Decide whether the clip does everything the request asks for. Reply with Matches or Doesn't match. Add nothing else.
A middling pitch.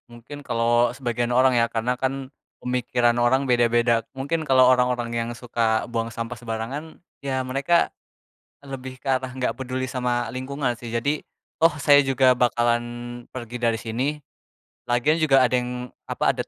Doesn't match